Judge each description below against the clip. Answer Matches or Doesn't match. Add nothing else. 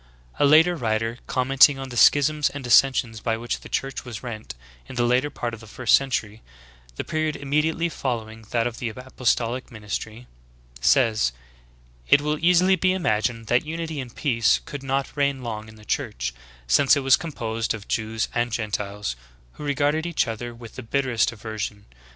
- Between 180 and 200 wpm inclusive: Matches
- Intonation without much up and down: Doesn't match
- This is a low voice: Matches